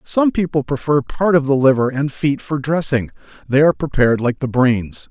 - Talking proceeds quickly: No, average, 190 wpm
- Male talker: Yes, male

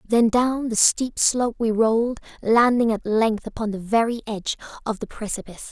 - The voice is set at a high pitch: Yes, high, 225 Hz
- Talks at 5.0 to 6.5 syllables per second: Yes, 5.2 syllables/s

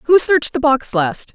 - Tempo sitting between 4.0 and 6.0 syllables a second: Yes, 4.6 syllables/s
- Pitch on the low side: No, very high, 270 Hz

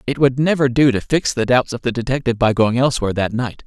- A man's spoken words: Yes, male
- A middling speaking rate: No, fast, 260 wpm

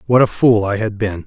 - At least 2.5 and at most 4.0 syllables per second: No, 5.4 syllables/s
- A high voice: No, low, 105 Hz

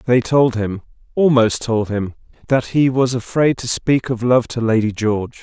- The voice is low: Yes, low, 120 Hz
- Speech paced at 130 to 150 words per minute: No, average, 165 wpm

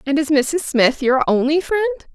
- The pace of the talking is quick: No, average, 195 wpm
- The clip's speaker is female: Yes, female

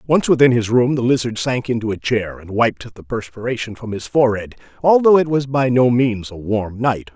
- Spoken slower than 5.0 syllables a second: No, 5.2 syllables/s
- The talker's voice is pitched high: No, low, 120 Hz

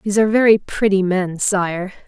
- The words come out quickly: No, average, 175 wpm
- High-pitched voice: Yes, high, 195 Hz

